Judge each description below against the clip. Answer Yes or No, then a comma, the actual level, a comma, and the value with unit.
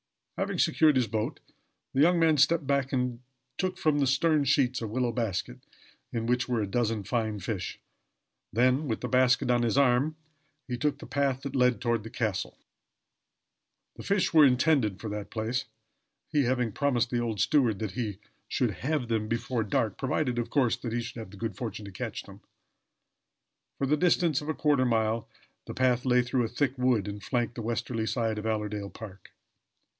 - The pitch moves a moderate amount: Yes, average, 3.4 semitones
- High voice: No, low, 120 Hz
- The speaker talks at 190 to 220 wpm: Yes, average, 200 wpm